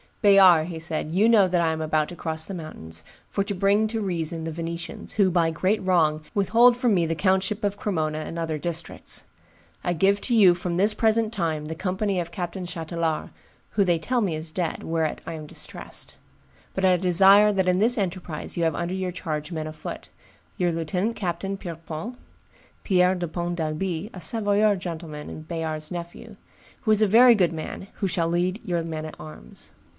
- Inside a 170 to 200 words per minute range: Yes, average, 195 wpm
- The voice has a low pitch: No, medium, 175 Hz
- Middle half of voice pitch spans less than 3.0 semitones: No, average, 3.4 semitones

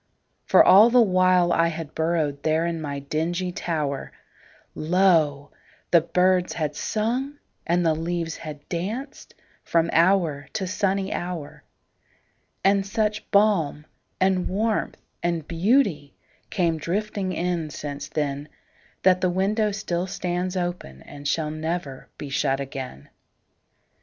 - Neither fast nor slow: No, slow, 110 wpm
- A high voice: No, medium, 175 Hz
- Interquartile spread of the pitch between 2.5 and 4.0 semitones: Yes, average, 3.6 semitones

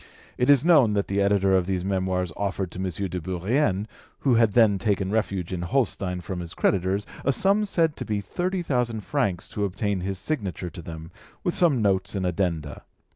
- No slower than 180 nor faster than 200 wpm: Yes, average, 195 wpm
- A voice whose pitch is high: No, low, 100 Hz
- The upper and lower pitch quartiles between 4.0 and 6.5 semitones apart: Yes, average, 4.3 semitones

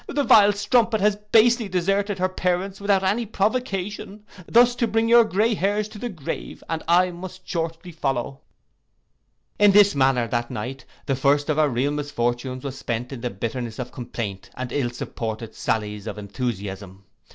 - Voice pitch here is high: No, medium, 165 Hz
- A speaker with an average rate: Yes, average, 170 wpm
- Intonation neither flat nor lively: No, wide, 8.9 semitones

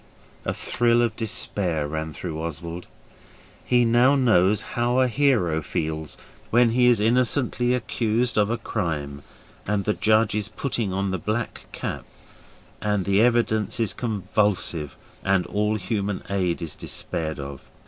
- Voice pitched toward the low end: Yes, low, 105 Hz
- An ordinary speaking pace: Yes, average, 145 wpm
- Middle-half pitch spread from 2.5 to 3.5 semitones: No, average, 5.2 semitones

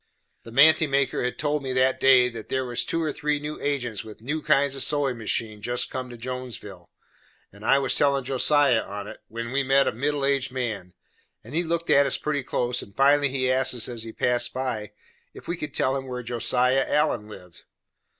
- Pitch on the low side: Yes, low, 130 Hz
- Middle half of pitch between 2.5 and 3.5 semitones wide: Yes, average, 3.1 semitones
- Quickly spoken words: Yes, fast, 215 wpm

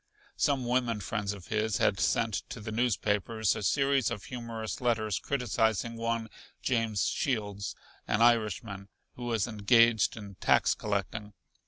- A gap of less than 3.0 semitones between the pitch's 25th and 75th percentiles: Yes, narrow, 2.4 semitones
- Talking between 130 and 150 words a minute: Yes, average, 140 wpm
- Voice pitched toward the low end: Yes, low, 110 Hz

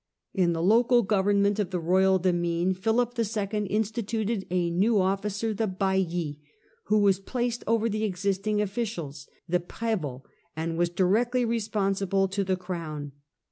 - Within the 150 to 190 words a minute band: No, average, 140 wpm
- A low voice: No, high, 195 Hz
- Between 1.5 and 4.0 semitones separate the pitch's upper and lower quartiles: Yes, average, 3.3 semitones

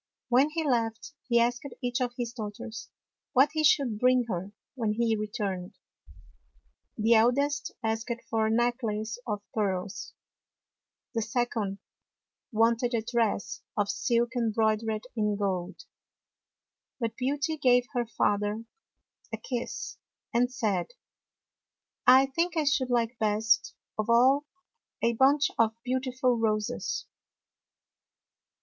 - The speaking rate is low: Yes, slow, 125 wpm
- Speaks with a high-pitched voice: Yes, high, 235 Hz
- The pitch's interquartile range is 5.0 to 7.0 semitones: No, average, 2.7 semitones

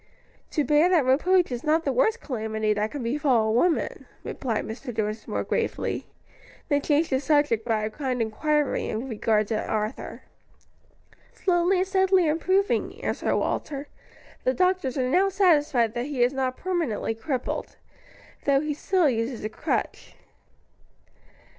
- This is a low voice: No, very high, 275 Hz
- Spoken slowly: No, average, 145 wpm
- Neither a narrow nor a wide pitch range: No, wide, 6.2 semitones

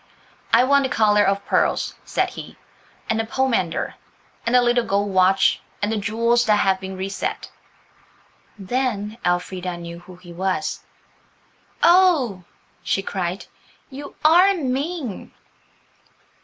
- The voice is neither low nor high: No, high, 210 Hz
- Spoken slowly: Yes, slow, 130 wpm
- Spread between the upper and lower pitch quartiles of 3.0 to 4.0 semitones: No, average, 5.2 semitones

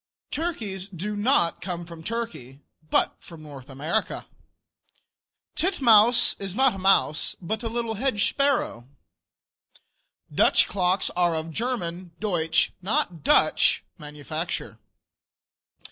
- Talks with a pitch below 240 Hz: Yes, high, 190 Hz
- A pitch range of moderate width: No, wide, 5.9 semitones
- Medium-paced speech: No, slow, 105 wpm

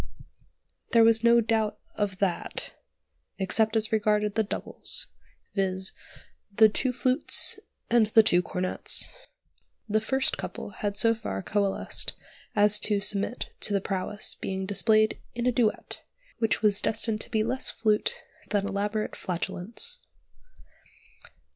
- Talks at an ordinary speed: No, slow, 130 wpm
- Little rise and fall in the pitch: Yes, narrow, 2.1 semitones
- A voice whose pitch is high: Yes, high, 215 Hz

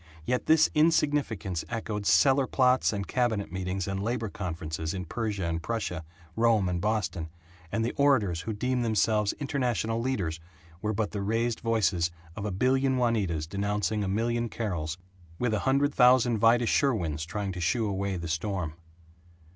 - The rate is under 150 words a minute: No, average, 160 wpm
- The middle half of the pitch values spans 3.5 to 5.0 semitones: Yes, average, 4.5 semitones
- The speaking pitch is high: No, low, 105 Hz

